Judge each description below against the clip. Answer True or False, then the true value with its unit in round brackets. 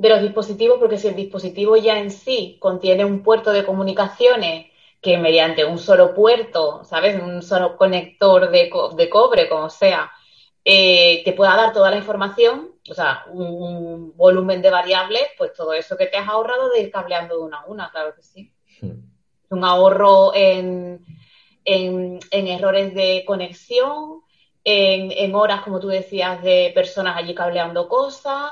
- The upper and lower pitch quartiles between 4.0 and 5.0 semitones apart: False (3.5 semitones)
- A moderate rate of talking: True (170 wpm)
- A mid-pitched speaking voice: False (195 Hz)